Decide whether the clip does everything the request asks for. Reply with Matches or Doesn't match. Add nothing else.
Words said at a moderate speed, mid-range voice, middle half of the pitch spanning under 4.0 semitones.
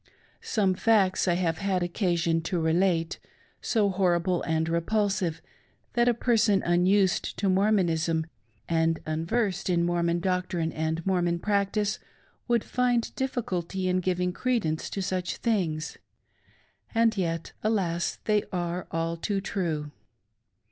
Doesn't match